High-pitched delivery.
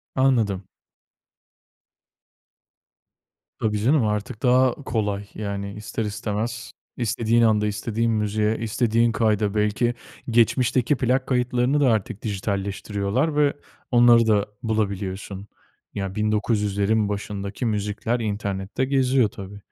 No: low, 110 Hz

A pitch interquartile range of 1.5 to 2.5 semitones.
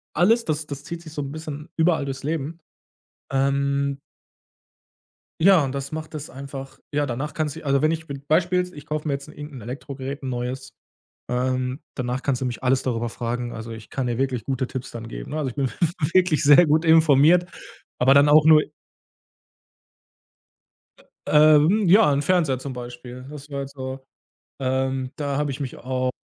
No: average, 2.9 semitones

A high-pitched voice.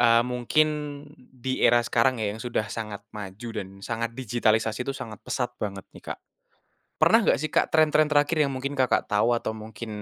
No: low, 120 Hz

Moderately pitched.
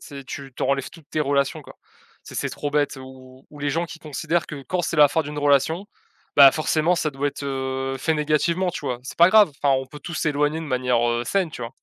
Yes: medium, 145 Hz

